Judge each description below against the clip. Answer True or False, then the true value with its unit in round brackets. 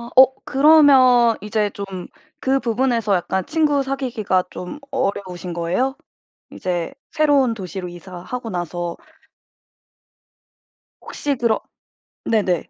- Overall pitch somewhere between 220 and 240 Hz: True (225 Hz)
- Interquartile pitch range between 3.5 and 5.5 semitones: False (6.5 semitones)